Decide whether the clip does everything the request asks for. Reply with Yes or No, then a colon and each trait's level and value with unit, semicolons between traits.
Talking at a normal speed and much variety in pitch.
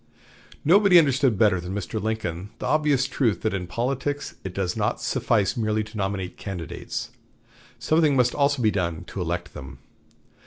Yes: average, 160 wpm; wide, 6.7 semitones